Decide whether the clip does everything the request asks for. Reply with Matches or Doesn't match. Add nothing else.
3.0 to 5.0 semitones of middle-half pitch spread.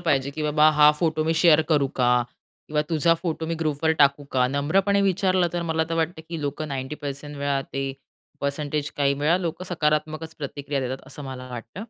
Doesn't match